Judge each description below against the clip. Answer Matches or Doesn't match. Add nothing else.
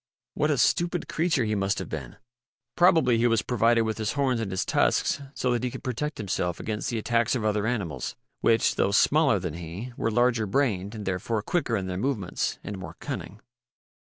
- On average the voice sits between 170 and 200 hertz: Doesn't match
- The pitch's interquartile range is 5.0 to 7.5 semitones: Doesn't match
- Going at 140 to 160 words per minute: Doesn't match